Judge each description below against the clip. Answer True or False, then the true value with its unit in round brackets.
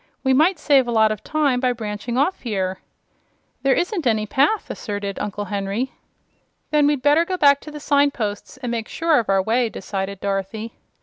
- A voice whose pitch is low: False (240 Hz)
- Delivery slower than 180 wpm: False (185 wpm)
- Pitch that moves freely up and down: True (5.8 semitones)